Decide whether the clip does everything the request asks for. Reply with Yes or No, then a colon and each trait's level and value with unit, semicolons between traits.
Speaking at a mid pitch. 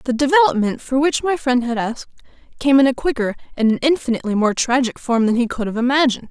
No: very high, 255 Hz